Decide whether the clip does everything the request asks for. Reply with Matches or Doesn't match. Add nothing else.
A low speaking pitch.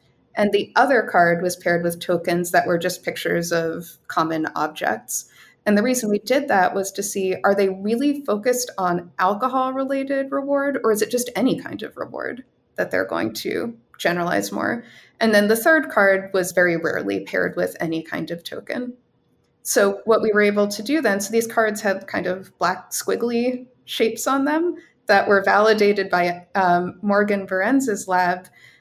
Doesn't match